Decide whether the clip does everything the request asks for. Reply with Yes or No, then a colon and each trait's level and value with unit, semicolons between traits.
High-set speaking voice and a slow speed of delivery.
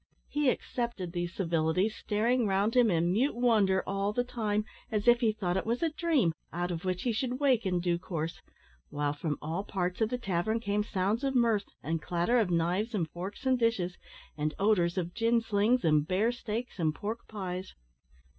No: high, 205 Hz; average, 195 wpm